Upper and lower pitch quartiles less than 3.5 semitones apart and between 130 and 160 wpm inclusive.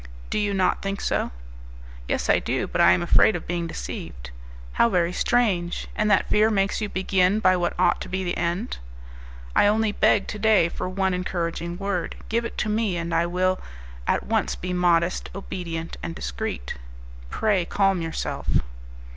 No: average, 2.9 semitones; average, 180 wpm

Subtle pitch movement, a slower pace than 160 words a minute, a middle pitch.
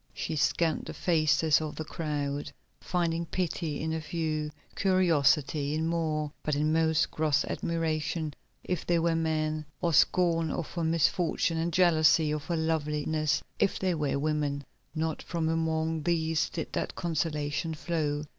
Yes: narrow, 1.5 semitones; average, 150 wpm; medium, 160 Hz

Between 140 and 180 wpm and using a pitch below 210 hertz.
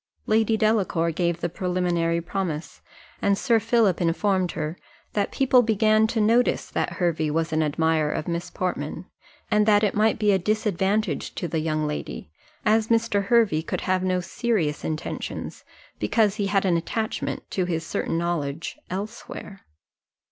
Yes: average, 160 wpm; medium, 185 Hz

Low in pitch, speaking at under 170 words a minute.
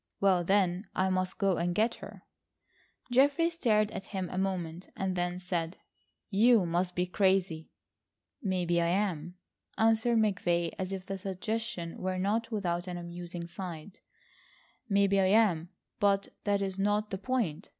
No: high, 190 Hz; average, 150 wpm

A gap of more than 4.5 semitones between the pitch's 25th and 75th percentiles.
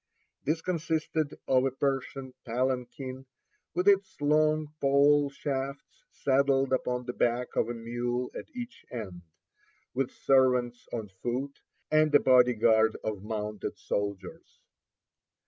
No: average, 3.2 semitones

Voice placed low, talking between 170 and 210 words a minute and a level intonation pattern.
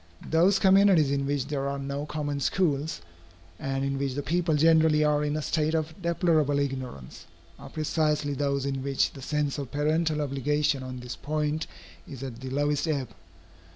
No: medium, 145 Hz; average, 175 wpm; narrow, 2.1 semitones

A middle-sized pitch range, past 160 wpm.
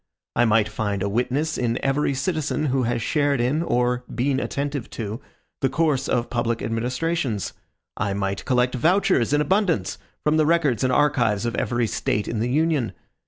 Yes: average, 4.3 semitones; average, 170 wpm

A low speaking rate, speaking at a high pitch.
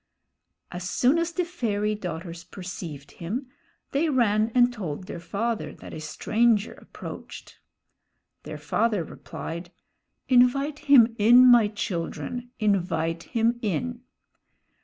Yes: slow, 115 wpm; high, 215 Hz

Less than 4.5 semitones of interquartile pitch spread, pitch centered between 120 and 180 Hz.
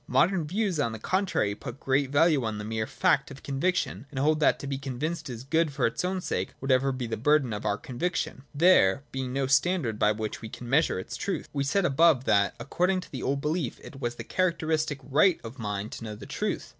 No: average, 5.3 semitones; low, 135 Hz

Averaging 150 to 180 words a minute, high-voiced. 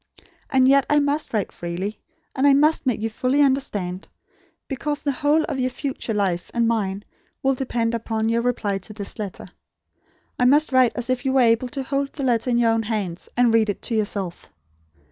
No: fast, 205 wpm; high, 240 Hz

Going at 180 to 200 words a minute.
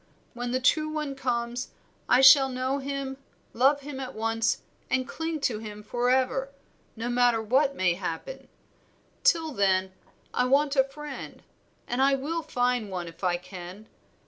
No: average, 155 wpm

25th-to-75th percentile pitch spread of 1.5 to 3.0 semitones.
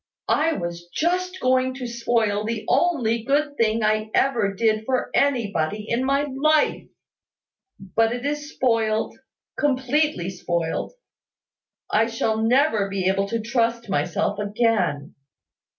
No: average, 4.4 semitones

